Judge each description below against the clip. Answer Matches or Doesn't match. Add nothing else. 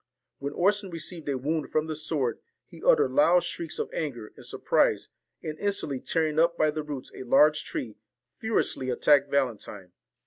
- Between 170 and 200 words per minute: Matches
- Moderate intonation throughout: Matches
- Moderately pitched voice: Matches